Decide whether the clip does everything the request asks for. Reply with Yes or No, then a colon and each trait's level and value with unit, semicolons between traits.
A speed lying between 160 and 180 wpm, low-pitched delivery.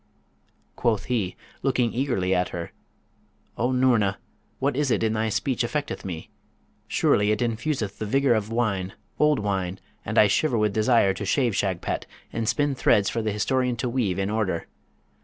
Yes: average, 170 wpm; low, 110 Hz